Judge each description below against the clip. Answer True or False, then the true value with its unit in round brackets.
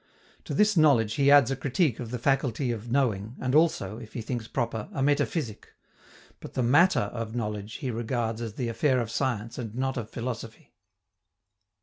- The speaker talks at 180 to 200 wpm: True (185 wpm)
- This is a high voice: False (120 Hz)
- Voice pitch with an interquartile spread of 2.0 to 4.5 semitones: True (3.2 semitones)